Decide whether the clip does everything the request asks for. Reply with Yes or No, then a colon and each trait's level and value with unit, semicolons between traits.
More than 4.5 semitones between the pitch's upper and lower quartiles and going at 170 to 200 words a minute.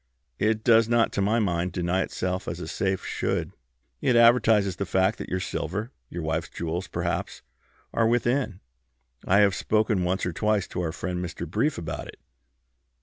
No: average, 3.8 semitones; average, 175 wpm